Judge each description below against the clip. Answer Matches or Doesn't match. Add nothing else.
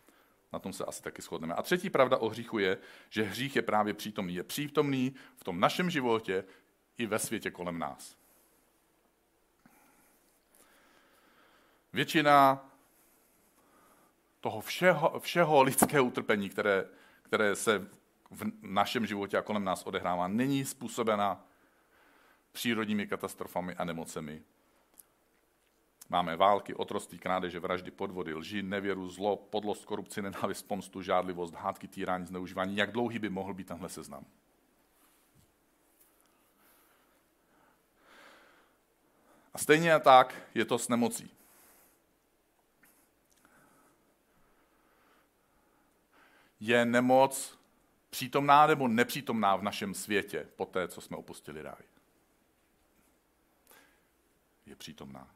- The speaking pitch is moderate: Doesn't match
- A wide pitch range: Matches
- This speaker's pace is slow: Matches